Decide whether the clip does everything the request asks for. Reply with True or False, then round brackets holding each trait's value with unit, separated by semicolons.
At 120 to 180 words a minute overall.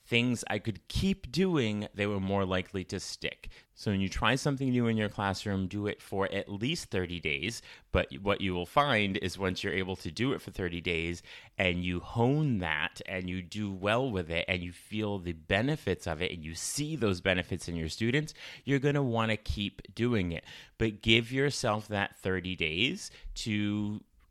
False (200 wpm)